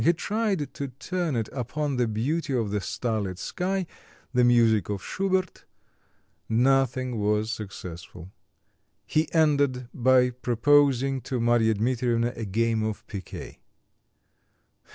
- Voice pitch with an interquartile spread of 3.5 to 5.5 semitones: Yes, average, 4.4 semitones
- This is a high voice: No, low, 125 Hz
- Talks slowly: Yes, slow, 120 wpm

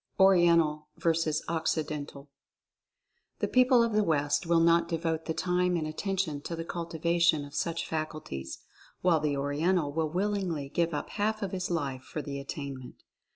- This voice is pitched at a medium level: Yes, medium, 165 Hz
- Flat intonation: No, average, 3.0 semitones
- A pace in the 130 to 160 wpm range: Yes, average, 155 wpm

